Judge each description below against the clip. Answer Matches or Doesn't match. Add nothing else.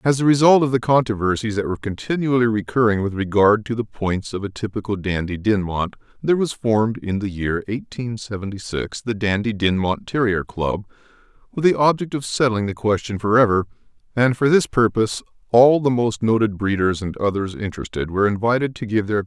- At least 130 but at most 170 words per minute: Doesn't match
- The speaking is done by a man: Matches